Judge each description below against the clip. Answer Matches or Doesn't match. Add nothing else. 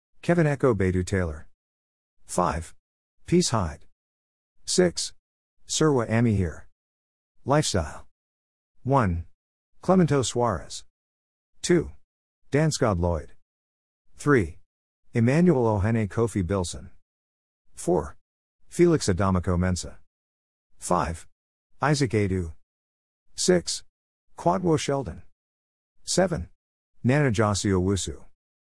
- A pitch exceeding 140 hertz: Doesn't match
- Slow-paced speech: Matches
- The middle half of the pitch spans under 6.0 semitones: Doesn't match